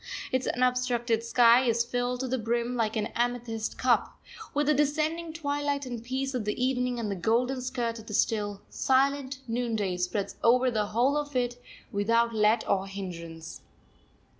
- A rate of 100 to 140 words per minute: No, average, 165 wpm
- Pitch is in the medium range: No, high, 240 Hz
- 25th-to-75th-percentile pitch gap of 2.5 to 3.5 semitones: Yes, average, 2.8 semitones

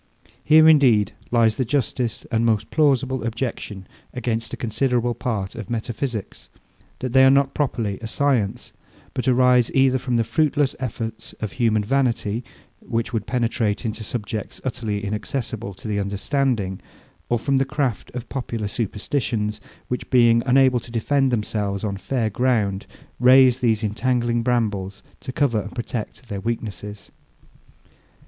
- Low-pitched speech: Yes, low, 115 Hz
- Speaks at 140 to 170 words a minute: Yes, average, 145 wpm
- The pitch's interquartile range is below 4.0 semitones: Yes, average, 3.3 semitones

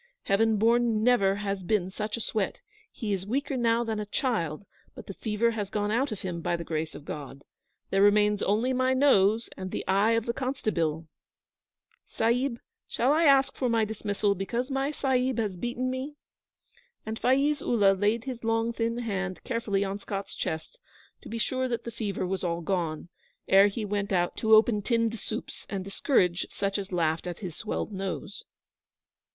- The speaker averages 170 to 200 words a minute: Yes, average, 185 wpm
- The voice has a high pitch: Yes, high, 215 Hz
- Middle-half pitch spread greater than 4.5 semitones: No, average, 3.5 semitones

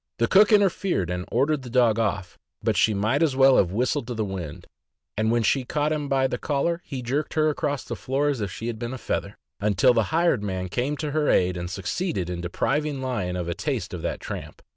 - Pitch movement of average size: No, wide, 6.6 semitones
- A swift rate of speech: Yes, fast, 240 wpm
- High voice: No, low, 125 Hz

